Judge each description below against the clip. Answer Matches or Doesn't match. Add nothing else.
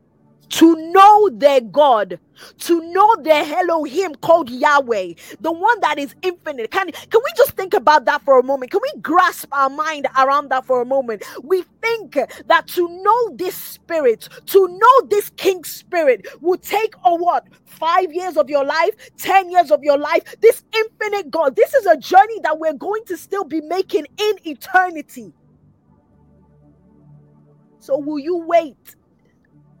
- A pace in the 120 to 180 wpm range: Matches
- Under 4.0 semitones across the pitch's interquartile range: Doesn't match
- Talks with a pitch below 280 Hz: Doesn't match